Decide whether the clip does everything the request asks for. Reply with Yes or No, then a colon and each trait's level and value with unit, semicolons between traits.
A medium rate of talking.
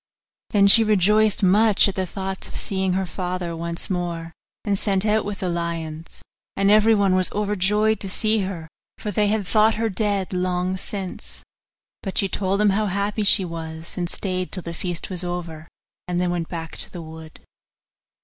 Yes: average, 185 wpm